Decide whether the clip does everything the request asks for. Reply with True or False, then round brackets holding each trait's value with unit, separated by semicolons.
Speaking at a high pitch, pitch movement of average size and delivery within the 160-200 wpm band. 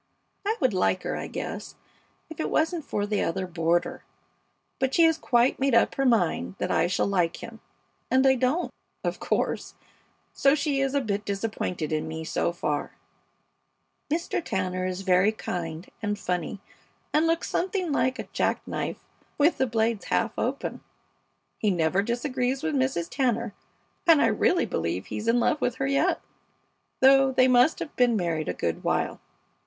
False (235 Hz; 6.9 semitones; 170 wpm)